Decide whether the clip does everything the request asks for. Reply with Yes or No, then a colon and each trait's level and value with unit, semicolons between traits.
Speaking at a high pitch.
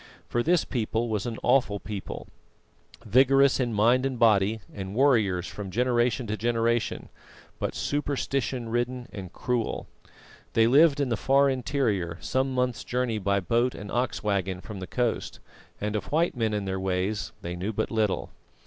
No: low, 115 Hz